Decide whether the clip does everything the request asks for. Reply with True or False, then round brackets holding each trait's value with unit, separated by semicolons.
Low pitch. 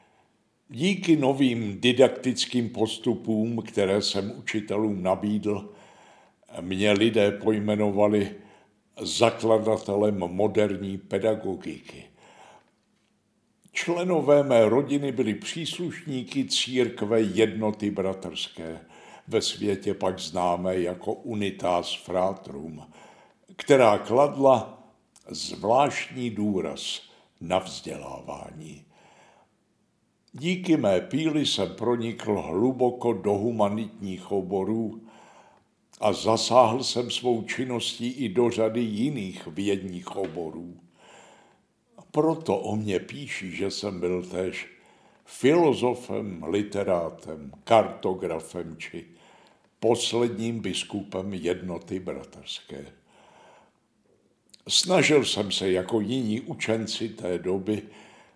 True (105 Hz)